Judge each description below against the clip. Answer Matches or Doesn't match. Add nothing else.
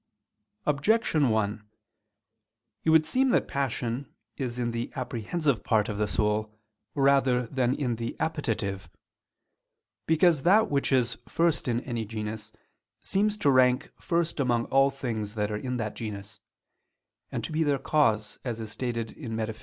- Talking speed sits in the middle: Matches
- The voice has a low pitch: Matches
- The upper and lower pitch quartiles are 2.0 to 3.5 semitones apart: Doesn't match